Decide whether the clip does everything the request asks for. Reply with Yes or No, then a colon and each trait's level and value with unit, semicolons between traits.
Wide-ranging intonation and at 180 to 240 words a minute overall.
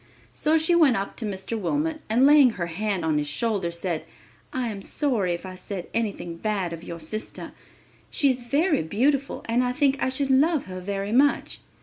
Yes: wide, 6.9 semitones; average, 200 wpm